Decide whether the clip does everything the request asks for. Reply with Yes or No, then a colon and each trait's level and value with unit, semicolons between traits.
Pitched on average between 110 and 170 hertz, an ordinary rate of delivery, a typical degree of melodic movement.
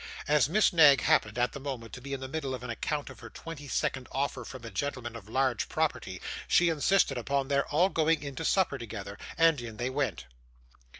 No: low, 135 Hz; fast, 220 wpm; average, 3.7 semitones